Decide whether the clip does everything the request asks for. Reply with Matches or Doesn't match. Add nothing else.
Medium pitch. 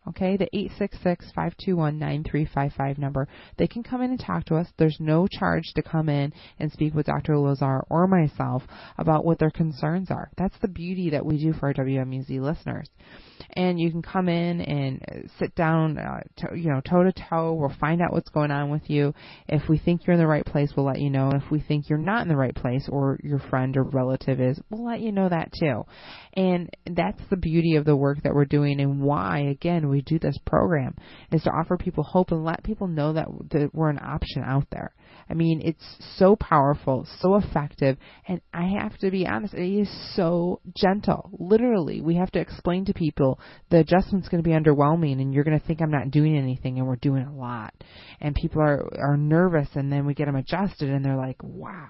Matches